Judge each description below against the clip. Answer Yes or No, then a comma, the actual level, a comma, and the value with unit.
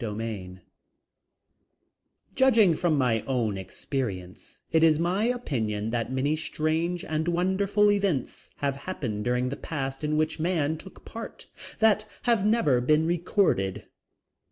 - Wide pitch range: Yes, wide, 7.1 semitones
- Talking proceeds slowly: Yes, slow, 130 wpm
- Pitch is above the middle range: No, medium, 155 Hz